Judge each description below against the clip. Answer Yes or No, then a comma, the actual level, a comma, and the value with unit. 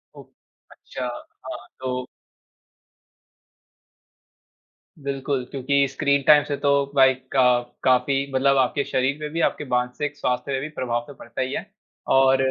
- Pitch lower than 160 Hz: Yes, low, 135 Hz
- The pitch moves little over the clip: Yes, narrow, 1.6 semitones